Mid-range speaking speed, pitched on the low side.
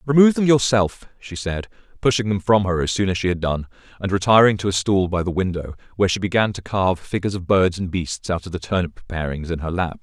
No: fast, 245 wpm; very low, 95 Hz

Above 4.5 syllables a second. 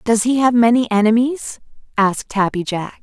Yes: 5.3 syllables/s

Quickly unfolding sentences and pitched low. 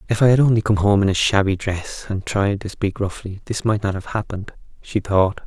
Yes: fast, 240 wpm; low, 100 Hz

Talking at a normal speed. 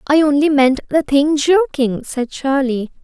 Yes: average, 160 wpm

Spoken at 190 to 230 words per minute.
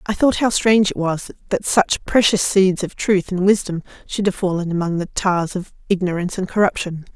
Yes: average, 200 wpm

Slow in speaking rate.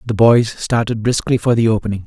No: fast, 205 wpm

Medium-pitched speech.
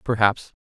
No: low, 110 Hz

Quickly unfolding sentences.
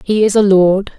Yes: fast, 245 wpm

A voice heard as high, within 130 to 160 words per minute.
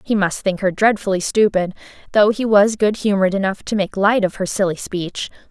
No: high, 200 Hz; fast, 205 wpm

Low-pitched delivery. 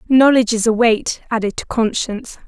No: high, 230 Hz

